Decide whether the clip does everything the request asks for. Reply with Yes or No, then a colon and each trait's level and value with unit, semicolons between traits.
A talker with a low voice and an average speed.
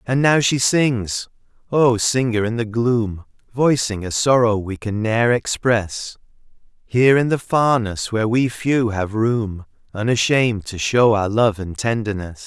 Yes: low, 115 Hz; average, 155 wpm